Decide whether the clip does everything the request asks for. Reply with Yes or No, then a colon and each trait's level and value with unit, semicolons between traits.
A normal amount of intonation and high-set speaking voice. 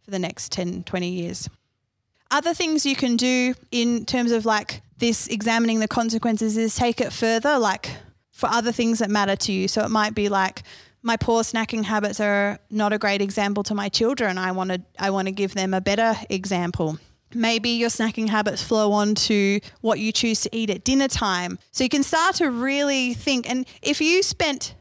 Yes: average, 3.1 semitones; high, 220 Hz